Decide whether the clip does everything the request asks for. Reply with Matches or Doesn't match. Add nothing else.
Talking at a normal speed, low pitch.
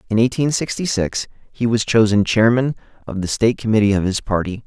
Matches